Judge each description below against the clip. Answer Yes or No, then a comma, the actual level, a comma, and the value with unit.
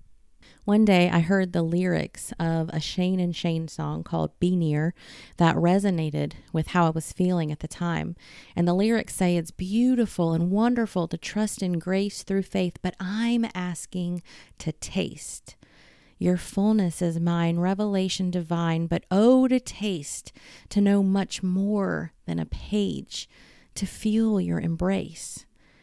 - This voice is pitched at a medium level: Yes, medium, 180 Hz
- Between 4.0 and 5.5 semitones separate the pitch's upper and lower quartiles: No, average, 2.9 semitones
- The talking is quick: No, average, 150 wpm